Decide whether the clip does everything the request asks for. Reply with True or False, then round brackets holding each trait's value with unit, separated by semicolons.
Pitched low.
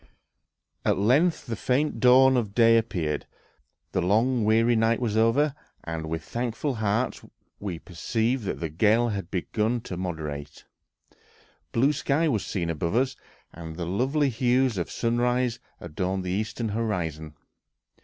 True (110 Hz)